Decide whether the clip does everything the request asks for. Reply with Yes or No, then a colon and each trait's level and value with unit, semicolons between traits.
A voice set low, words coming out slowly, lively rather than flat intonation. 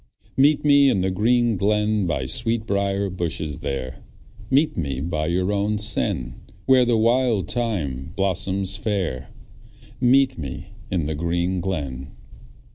Yes: very low, 95 Hz; slow, 130 wpm; wide, 6.3 semitones